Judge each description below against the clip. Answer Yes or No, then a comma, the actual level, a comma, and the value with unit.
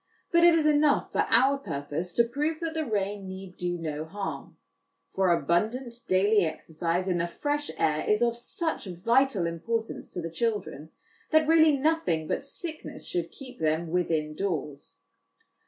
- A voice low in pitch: No, high, 200 Hz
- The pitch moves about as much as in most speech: No, wide, 8.6 semitones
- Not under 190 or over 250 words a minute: No, average, 160 wpm